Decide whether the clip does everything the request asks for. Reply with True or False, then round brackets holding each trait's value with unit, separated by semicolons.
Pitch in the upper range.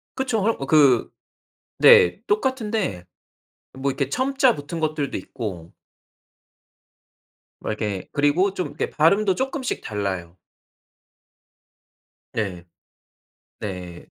False (145 Hz)